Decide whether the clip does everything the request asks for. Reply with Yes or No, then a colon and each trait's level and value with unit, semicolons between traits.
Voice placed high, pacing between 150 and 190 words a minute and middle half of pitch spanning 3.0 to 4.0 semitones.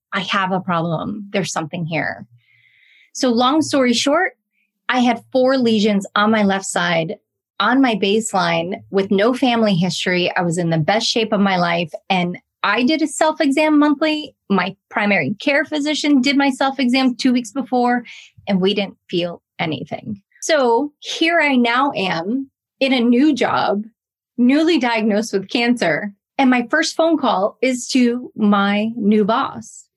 No: high, 225 Hz; average, 160 wpm; average, 5.2 semitones